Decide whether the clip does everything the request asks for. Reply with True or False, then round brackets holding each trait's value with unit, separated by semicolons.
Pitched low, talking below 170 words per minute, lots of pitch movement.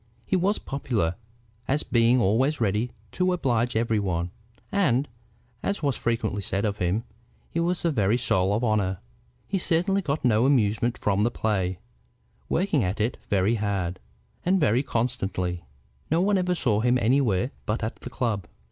True (115 Hz; 160 wpm; 5.7 semitones)